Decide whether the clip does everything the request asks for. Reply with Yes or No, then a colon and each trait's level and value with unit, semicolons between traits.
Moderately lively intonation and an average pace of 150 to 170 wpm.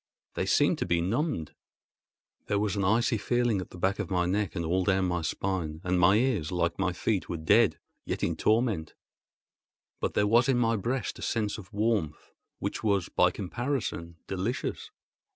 No: average, 4.3 semitones; average, 185 wpm